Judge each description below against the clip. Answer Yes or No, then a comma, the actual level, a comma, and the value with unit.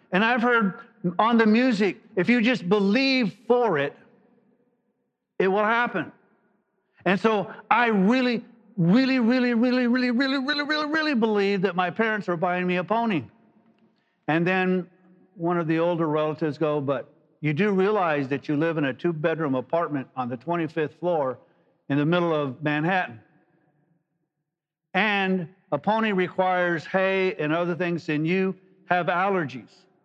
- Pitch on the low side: No, medium, 185 Hz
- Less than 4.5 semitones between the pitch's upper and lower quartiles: No, wide, 5.5 semitones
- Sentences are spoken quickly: No, average, 155 wpm